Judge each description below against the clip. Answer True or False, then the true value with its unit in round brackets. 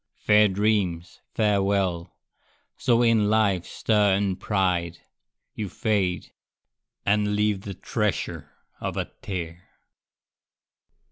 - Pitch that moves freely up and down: False (2.4 semitones)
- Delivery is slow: True (95 wpm)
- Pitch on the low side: True (100 Hz)